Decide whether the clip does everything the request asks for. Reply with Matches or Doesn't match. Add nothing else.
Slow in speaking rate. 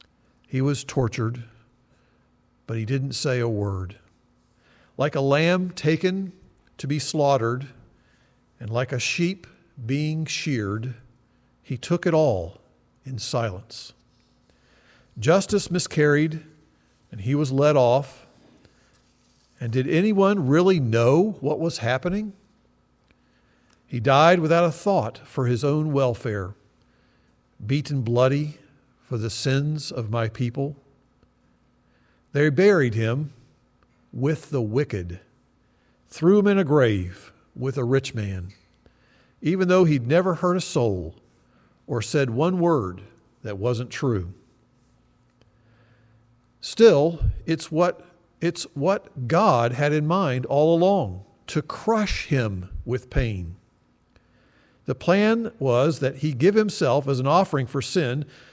Matches